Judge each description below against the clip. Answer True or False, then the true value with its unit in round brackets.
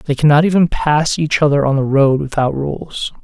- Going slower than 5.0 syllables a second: True (4.8 syllables/s)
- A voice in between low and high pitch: True (145 Hz)